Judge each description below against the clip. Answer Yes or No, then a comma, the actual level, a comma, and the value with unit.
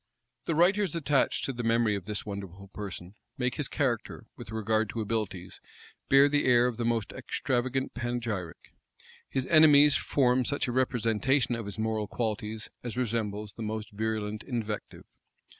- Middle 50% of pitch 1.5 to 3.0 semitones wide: No, average, 3.4 semitones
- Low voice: Yes, low, 115 Hz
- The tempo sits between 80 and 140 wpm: No, average, 160 wpm